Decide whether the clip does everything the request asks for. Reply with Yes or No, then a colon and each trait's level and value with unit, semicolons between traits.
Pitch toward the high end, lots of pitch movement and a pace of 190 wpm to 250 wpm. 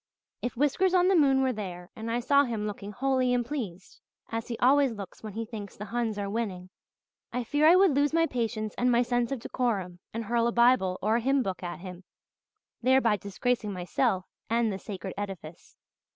No: high, 230 Hz; average, 4.2 semitones; average, 200 wpm